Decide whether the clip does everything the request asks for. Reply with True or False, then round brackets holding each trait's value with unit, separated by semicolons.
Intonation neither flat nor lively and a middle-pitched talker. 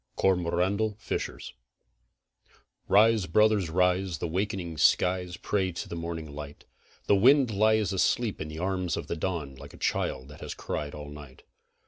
False (4.2 semitones; 90 Hz)